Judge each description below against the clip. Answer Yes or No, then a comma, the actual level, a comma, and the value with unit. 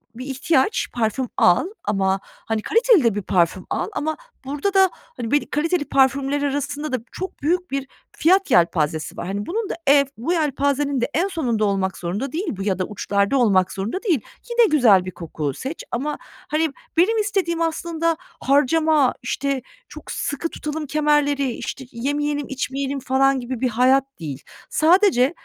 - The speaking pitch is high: Yes, very high, 275 Hz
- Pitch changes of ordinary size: No, wide, 5.7 semitones